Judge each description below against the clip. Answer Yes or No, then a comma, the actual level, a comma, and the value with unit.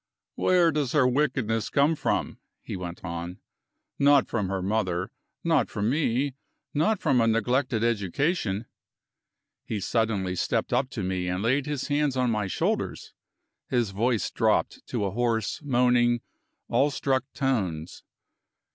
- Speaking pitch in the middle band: No, low, 120 Hz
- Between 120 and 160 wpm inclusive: Yes, slow, 135 wpm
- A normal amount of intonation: No, wide, 5.7 semitones